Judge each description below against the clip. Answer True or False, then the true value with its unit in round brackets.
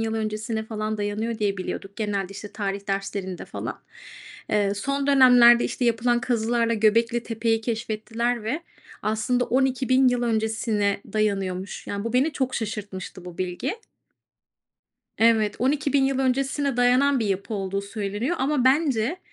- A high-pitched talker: True (225 Hz)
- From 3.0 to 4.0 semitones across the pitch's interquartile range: True (3.3 semitones)